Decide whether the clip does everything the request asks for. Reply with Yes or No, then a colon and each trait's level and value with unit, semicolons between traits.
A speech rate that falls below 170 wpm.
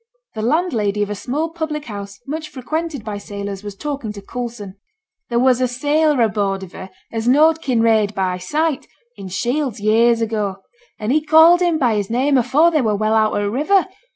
No: average, 195 wpm